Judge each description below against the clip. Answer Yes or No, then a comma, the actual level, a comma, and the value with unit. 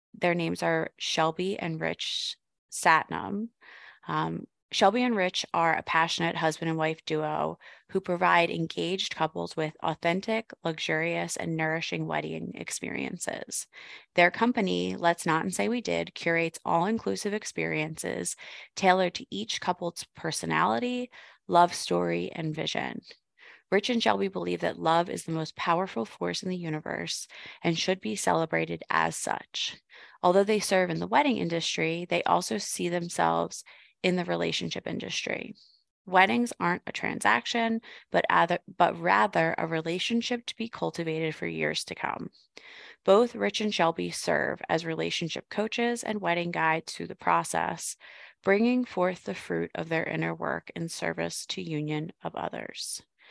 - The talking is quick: No, average, 145 wpm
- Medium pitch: Yes, medium, 165 Hz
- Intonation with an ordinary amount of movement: Yes, average, 4.0 semitones